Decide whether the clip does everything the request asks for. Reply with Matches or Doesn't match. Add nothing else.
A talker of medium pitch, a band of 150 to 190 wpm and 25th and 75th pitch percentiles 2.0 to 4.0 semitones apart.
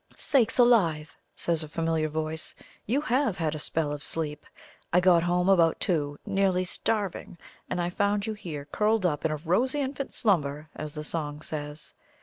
Doesn't match